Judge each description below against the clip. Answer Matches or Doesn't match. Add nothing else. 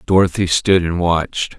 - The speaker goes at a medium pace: Matches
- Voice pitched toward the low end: Matches